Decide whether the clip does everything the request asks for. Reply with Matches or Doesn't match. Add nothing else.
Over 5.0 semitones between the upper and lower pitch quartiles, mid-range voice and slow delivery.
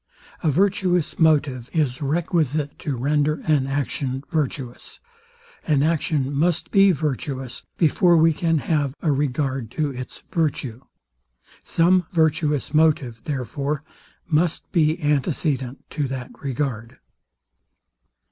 Doesn't match